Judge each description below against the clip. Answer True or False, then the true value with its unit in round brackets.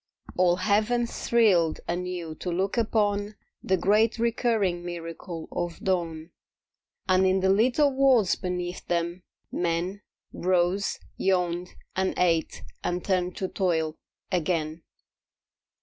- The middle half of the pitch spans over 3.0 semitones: False (2.7 semitones)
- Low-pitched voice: False (185 Hz)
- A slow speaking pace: True (115 wpm)